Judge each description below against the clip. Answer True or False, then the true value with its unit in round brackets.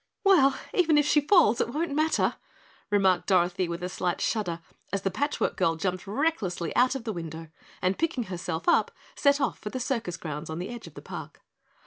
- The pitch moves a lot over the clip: True (8.0 semitones)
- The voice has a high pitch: True (205 Hz)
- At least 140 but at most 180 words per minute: False (205 wpm)